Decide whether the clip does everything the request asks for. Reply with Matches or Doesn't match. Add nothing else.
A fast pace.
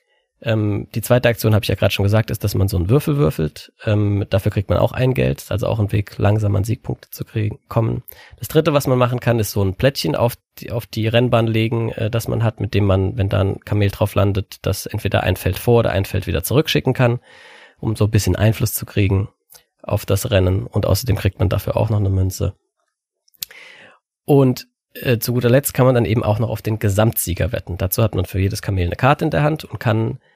Matches